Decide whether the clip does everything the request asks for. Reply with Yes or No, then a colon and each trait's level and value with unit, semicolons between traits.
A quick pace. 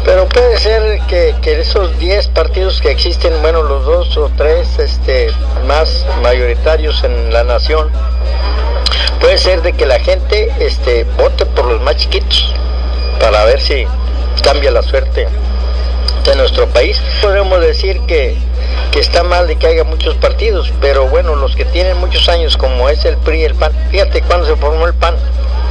No: average, 170 wpm